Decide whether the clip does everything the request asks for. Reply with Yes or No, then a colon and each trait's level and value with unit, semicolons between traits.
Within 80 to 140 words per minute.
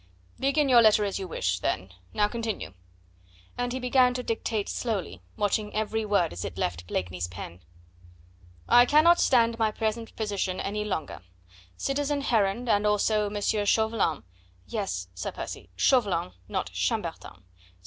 No: average, 150 wpm